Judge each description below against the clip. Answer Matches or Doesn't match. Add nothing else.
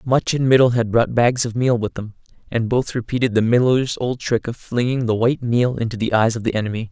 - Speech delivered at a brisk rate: Matches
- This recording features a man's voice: Matches